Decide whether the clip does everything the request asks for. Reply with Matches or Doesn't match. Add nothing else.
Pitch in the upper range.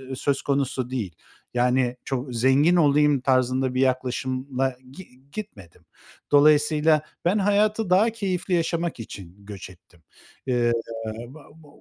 Doesn't match